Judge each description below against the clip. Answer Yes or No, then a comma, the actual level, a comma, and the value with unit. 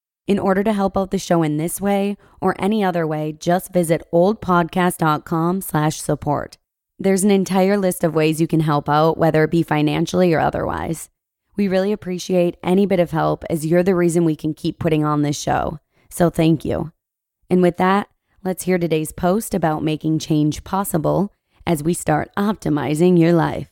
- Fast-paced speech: No, average, 180 wpm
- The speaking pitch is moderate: Yes, medium, 175 Hz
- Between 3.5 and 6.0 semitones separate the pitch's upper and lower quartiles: No, average, 3.0 semitones